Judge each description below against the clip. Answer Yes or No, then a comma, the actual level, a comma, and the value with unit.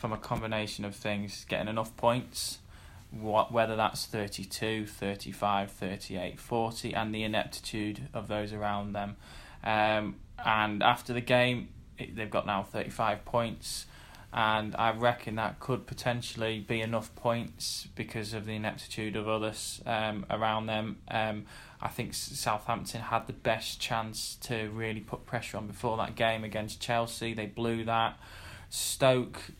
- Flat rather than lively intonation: Yes, narrow, 1.7 semitones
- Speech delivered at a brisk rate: No, average, 145 wpm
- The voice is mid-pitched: No, low, 110 Hz